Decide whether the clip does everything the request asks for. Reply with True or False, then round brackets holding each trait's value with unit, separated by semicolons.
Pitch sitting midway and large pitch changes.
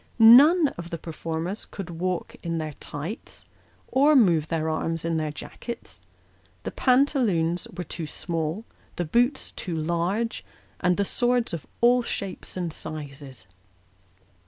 True (175 Hz; 6.4 semitones)